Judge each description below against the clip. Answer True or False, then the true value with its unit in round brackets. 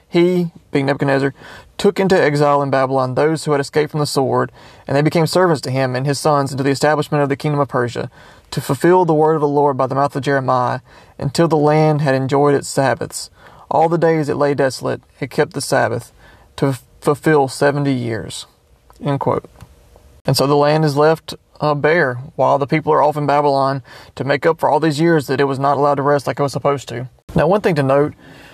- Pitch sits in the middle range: True (145 Hz)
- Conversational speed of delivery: False (225 wpm)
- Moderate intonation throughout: False (1.9 semitones)